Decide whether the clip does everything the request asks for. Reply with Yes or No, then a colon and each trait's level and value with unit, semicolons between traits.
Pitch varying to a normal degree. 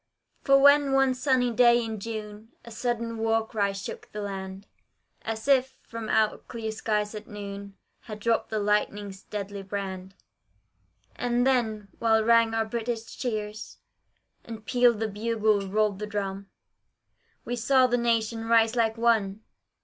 No: narrow, 2.1 semitones